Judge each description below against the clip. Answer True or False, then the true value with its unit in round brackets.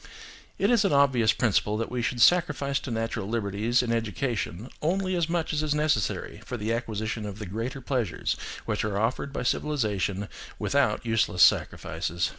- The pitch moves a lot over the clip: False (4.9 semitones)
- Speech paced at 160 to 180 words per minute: True (170 wpm)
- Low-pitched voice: True (115 Hz)